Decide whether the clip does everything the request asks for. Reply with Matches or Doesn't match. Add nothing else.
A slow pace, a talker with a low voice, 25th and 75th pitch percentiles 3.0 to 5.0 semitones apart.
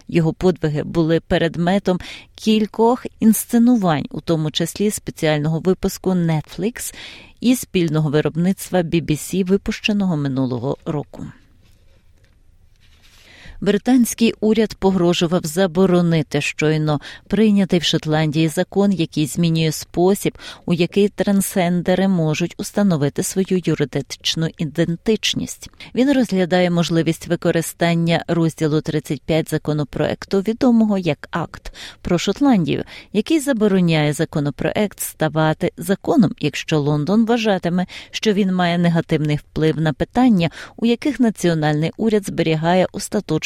Doesn't match